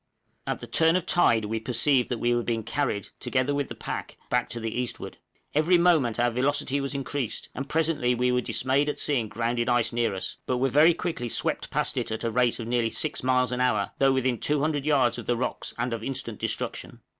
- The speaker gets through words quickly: Yes, fast, 225 wpm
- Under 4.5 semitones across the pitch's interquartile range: Yes, average, 3.3 semitones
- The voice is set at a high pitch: No, low, 125 Hz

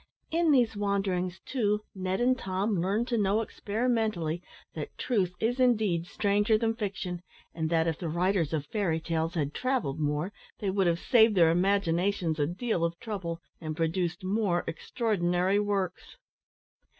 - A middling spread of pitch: Yes, average, 4.2 semitones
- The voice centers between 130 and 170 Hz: No, high, 190 Hz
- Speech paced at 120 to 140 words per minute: No, average, 155 wpm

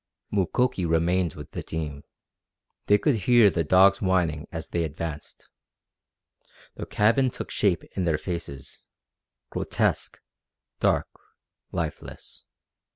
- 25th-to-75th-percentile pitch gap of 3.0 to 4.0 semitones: Yes, average, 3.7 semitones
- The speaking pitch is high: No, very low, 85 Hz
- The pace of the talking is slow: Yes, slow, 110 wpm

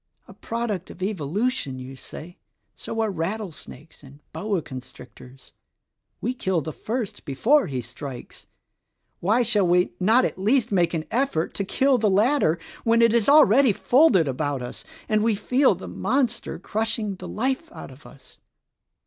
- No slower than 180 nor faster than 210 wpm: No, average, 155 wpm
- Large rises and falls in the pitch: Yes, wide, 6.9 semitones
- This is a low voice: No, high, 200 Hz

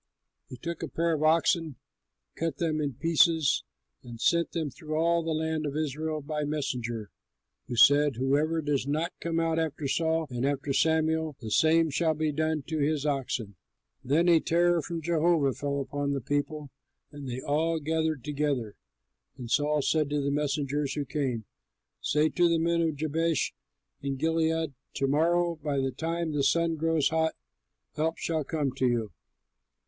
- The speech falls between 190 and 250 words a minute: No, average, 170 wpm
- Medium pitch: Yes, medium, 155 Hz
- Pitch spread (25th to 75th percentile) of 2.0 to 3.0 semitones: Yes, narrow, 2.5 semitones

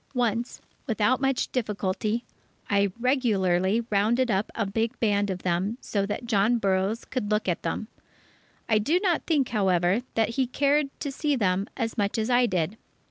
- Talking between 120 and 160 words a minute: No, average, 170 wpm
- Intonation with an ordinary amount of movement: Yes, average, 3.8 semitones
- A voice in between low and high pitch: No, high, 220 Hz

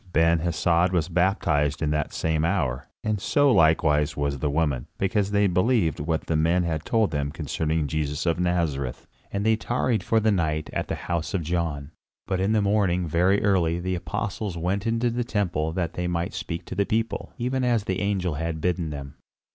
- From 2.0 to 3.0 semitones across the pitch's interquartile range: No, average, 4.2 semitones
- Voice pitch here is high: No, very low, 85 Hz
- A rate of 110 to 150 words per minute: No, average, 195 wpm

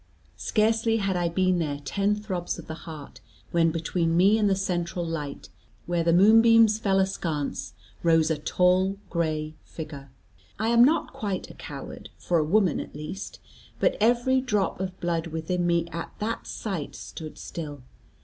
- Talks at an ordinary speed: Yes, average, 165 wpm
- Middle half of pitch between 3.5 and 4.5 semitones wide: Yes, average, 4.0 semitones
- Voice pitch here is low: No, medium, 175 Hz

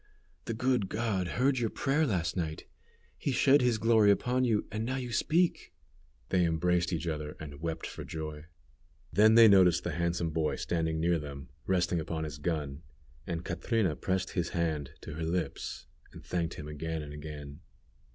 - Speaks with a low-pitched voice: Yes, very low, 85 Hz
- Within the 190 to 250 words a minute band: No, average, 175 wpm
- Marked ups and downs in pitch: Yes, wide, 5.7 semitones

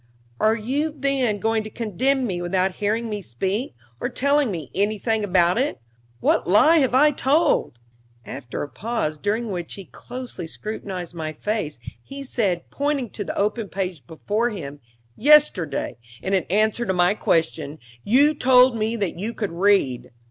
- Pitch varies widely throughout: Yes, wide, 5.7 semitones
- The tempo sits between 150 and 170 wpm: Yes, average, 160 wpm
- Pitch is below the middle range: No, high, 210 Hz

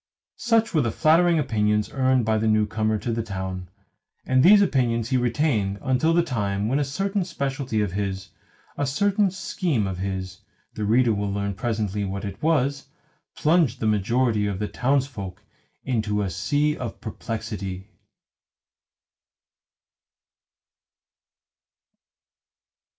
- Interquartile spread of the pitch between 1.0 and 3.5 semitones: No, wide, 5.6 semitones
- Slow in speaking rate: Yes, slow, 130 wpm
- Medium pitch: No, low, 115 Hz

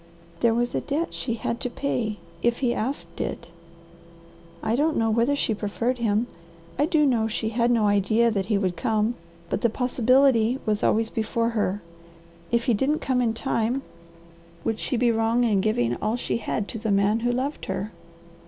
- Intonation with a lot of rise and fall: No, narrow, 2.4 semitones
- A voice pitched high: Yes, high, 230 Hz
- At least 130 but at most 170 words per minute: No, average, 190 wpm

